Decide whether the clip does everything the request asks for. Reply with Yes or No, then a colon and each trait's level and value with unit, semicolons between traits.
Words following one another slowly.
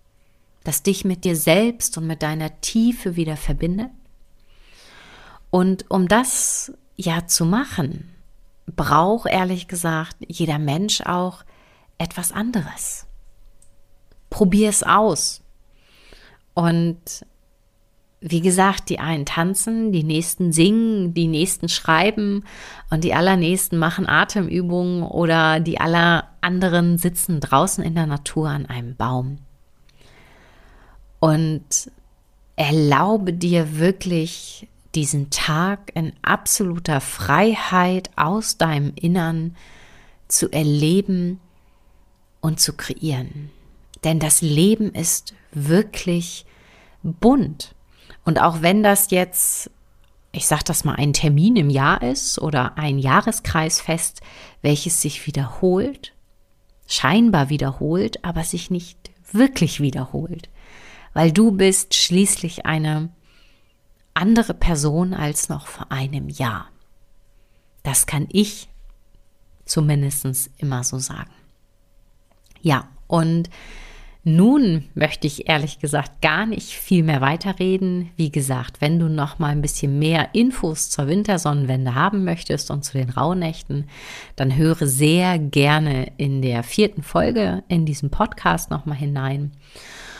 Yes: slow, 115 wpm